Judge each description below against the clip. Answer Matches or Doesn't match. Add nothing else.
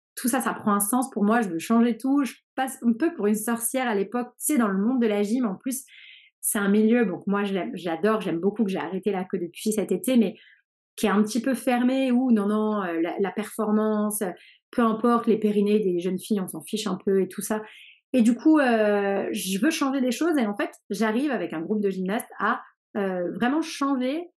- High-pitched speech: Matches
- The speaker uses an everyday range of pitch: Matches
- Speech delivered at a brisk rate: Matches